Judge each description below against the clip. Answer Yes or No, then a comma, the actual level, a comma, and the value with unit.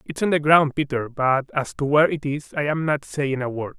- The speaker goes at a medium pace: No, fast, 270 wpm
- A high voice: No, medium, 145 Hz